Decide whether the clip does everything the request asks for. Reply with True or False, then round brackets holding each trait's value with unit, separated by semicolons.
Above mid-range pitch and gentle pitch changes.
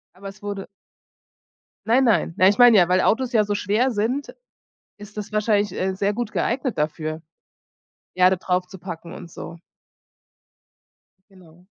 False (200 Hz; 3.1 semitones)